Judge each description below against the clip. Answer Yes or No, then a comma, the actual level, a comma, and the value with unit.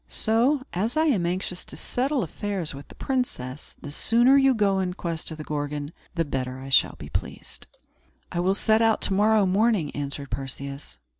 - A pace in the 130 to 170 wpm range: No, average, 190 wpm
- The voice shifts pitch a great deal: Yes, wide, 7.6 semitones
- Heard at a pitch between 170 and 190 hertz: Yes, medium, 185 Hz